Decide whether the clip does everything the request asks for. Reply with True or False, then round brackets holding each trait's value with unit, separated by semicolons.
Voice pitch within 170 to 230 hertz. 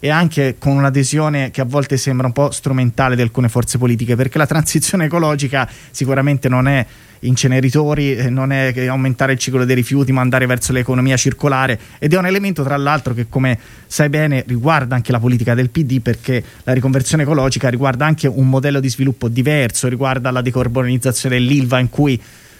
False (130 Hz)